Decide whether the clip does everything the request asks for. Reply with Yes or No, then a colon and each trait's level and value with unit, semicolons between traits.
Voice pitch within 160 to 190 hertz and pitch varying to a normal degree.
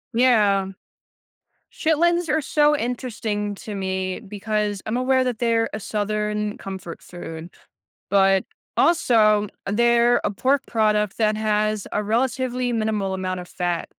No: high, 215 Hz; average, 3.4 semitones